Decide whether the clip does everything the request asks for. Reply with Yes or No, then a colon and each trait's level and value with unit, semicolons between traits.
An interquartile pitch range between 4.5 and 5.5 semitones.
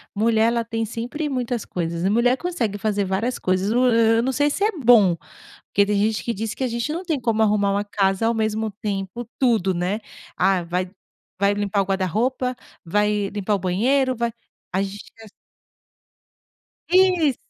No: average, 3.7 semitones